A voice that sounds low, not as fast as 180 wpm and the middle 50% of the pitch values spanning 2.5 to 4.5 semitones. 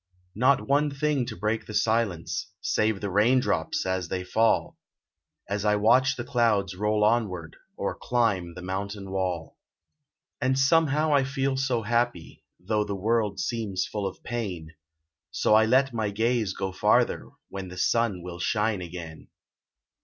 Yes: low, 105 Hz; average, 155 wpm; average, 4.2 semitones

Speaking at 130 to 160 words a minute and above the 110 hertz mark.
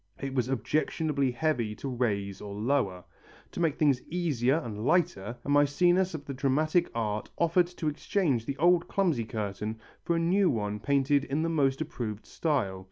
No: average, 170 wpm; medium, 140 Hz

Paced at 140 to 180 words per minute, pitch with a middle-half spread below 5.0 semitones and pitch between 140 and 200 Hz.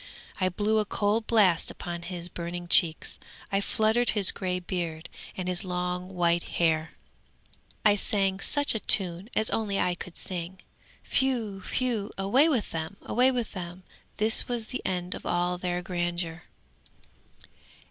Yes: average, 150 wpm; average, 3.6 semitones; medium, 185 Hz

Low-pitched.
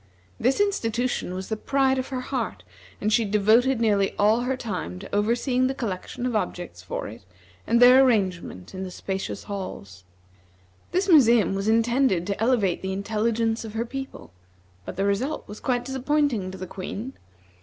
No: high, 225 Hz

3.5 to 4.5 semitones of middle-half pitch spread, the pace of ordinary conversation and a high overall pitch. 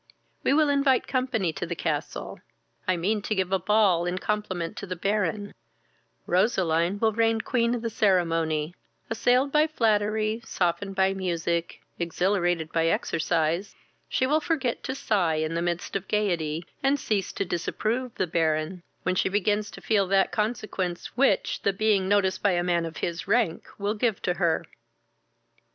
Yes: average, 4.2 semitones; average, 165 wpm; high, 195 Hz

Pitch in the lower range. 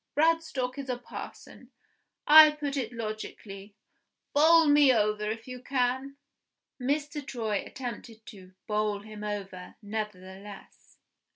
No: high, 230 Hz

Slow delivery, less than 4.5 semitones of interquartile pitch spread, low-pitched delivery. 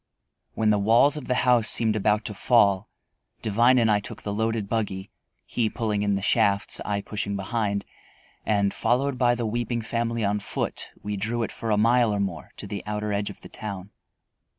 No: average, 195 wpm; narrow, 2.4 semitones; low, 105 Hz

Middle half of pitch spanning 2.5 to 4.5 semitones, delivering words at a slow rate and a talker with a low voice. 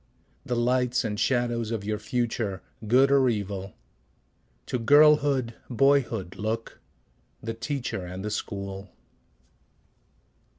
Yes: average, 3.7 semitones; slow, 110 wpm; low, 115 Hz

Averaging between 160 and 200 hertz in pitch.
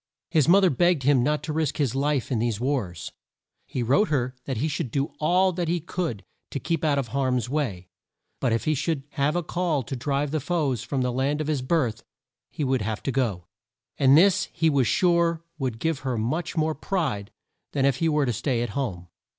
No: medium, 140 Hz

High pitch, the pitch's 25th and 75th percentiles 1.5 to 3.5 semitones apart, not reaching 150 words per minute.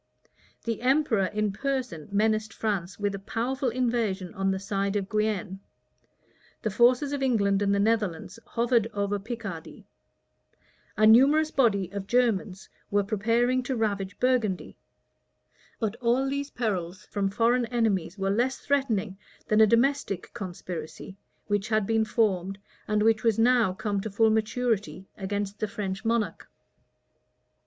Yes: high, 215 Hz; average, 3.2 semitones; average, 140 wpm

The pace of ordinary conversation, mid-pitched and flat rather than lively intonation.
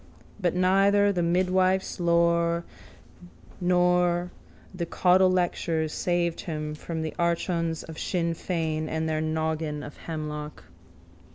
No: slow, 110 wpm; medium, 170 Hz; narrow, 2.1 semitones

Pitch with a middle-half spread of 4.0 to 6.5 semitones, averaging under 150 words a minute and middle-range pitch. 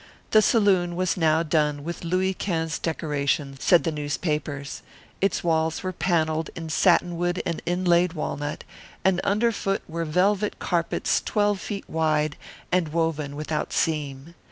No: average, 3.1 semitones; average, 140 wpm; medium, 165 Hz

